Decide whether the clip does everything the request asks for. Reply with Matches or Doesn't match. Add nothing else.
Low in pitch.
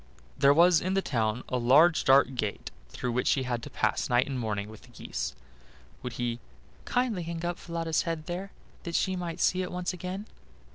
Doesn't match